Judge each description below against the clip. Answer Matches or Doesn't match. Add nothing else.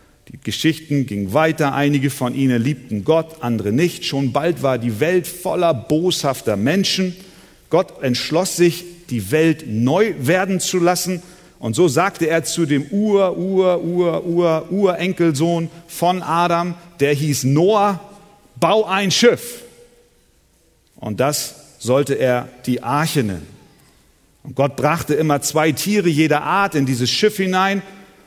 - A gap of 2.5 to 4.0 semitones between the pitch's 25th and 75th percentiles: Doesn't match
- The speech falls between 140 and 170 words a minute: Doesn't match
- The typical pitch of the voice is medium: Matches